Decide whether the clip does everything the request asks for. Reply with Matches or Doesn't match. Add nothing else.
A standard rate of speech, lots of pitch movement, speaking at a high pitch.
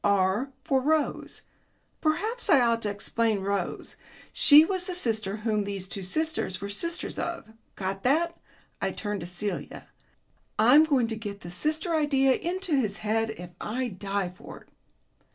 Matches